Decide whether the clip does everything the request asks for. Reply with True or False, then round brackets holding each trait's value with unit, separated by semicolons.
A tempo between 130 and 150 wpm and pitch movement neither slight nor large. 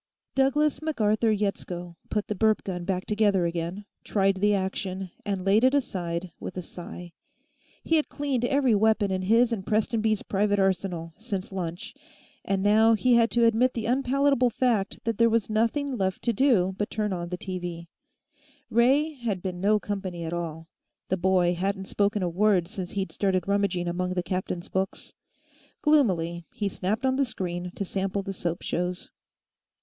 False (175 wpm; 3.9 semitones)